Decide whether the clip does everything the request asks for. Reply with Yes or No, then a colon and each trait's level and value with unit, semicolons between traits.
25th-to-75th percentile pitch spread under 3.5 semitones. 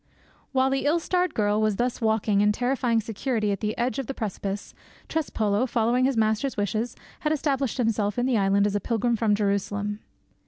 No: average, 3.8 semitones